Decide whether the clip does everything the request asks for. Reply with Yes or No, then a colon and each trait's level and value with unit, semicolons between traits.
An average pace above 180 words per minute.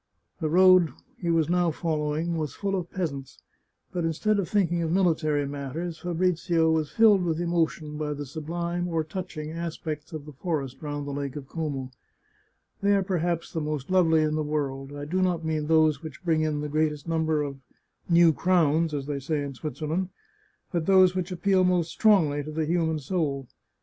Yes: average, 195 wpm